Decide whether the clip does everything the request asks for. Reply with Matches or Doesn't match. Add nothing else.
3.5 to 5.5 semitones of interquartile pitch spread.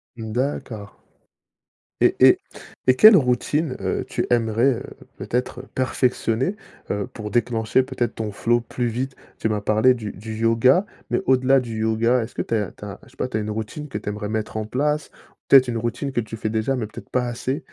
Doesn't match